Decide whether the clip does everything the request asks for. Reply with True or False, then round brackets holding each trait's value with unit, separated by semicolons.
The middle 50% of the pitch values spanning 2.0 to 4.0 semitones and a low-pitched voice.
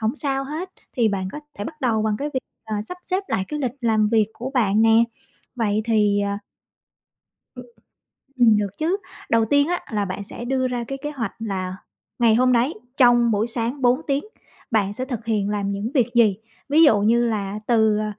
False (3.7 semitones; 230 Hz)